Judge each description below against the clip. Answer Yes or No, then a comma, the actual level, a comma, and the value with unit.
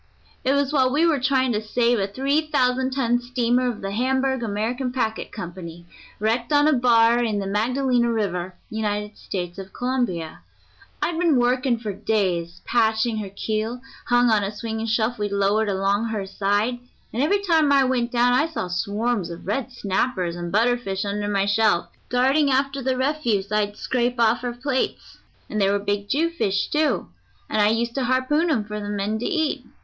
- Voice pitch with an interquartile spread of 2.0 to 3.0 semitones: No, average, 4.0 semitones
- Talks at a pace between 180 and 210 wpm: Yes, average, 185 wpm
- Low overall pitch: No, high, 230 Hz